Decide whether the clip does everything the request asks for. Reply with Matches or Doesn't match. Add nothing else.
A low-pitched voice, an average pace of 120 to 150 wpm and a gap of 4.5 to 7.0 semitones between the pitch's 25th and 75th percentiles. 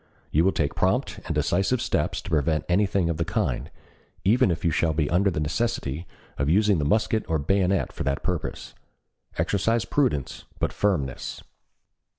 Doesn't match